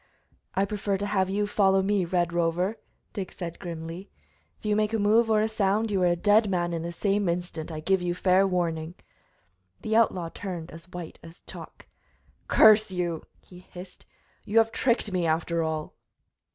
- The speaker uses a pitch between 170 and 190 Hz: Yes, medium, 185 Hz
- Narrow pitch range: No, average, 3.2 semitones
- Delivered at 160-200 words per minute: Yes, average, 185 wpm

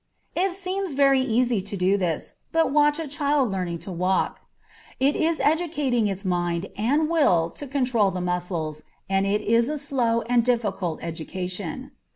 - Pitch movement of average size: No, wide, 7.7 semitones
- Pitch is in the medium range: No, high, 230 Hz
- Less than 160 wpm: No, average, 165 wpm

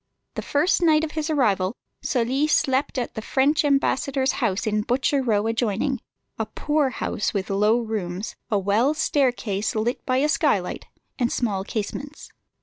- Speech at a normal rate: Yes, average, 155 wpm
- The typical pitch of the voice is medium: No, high, 245 Hz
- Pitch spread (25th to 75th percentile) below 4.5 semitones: No, average, 4.9 semitones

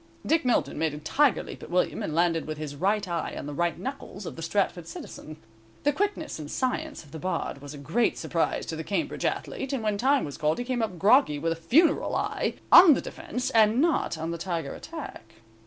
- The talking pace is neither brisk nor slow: No, fast, 225 wpm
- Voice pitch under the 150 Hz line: No, medium, 185 Hz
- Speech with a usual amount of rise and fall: No, wide, 8.4 semitones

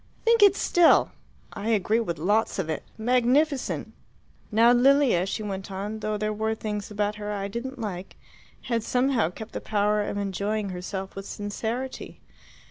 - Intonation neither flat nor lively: Yes, average, 3.0 semitones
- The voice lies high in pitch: Yes, high, 215 Hz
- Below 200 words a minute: Yes, average, 160 wpm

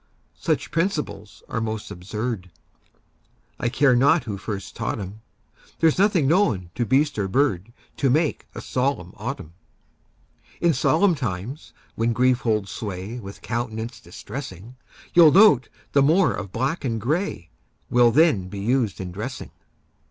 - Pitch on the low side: Yes, low, 120 Hz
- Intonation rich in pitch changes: Yes, wide, 5.8 semitones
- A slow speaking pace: No, average, 145 wpm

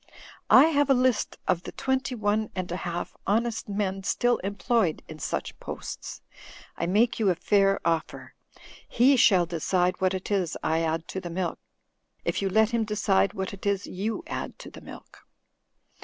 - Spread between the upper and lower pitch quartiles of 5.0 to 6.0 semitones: No, average, 3.7 semitones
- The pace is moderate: Yes, average, 180 wpm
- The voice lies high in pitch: Yes, high, 195 Hz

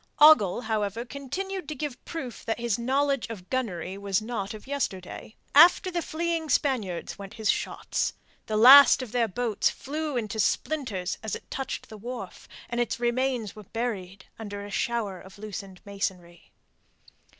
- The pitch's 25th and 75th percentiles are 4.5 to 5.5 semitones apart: Yes, average, 5.0 semitones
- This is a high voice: Yes, high, 230 Hz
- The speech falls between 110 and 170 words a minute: Yes, average, 160 wpm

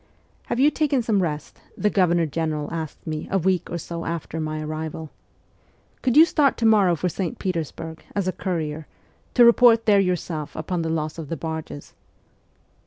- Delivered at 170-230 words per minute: Yes, average, 190 wpm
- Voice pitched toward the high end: No, medium, 170 Hz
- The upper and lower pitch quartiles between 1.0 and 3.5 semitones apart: No, average, 4.1 semitones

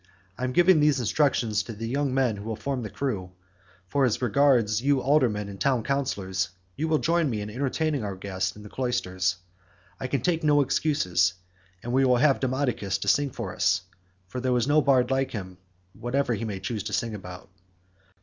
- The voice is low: Yes, low, 125 Hz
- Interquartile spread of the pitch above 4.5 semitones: Yes, average, 5.2 semitones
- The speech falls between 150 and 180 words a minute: No, average, 200 wpm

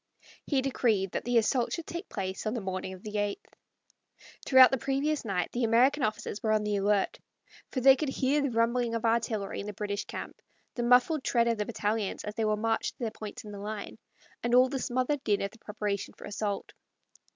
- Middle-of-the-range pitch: No, high, 225 Hz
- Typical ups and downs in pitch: Yes, average, 3.5 semitones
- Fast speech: Yes, fast, 220 wpm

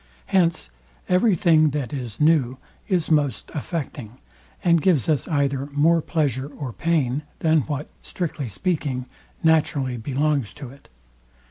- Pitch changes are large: No, average, 3.7 semitones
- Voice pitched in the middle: Yes, medium, 150 Hz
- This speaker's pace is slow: Yes, slow, 130 wpm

